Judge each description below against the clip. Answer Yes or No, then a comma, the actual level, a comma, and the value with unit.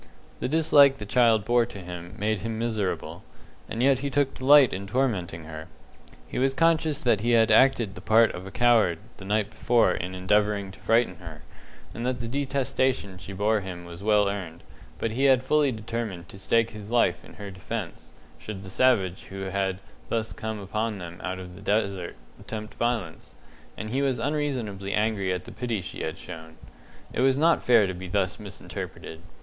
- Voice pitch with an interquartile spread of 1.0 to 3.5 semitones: No, average, 4.3 semitones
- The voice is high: No, low, 105 Hz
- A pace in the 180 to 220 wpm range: Yes, average, 190 wpm